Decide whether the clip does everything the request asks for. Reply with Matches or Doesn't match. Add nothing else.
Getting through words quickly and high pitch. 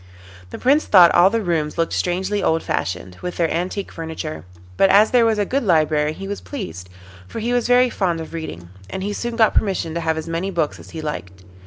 Doesn't match